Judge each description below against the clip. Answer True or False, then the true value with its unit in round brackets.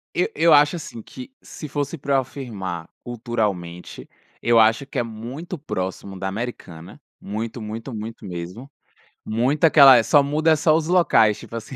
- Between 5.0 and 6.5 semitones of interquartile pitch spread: True (5.4 semitones)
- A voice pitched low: True (120 Hz)